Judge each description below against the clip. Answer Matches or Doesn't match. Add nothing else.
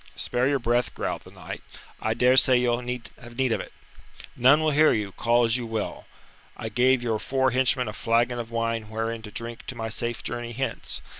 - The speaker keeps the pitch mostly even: Matches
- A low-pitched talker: Matches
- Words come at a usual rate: Doesn't match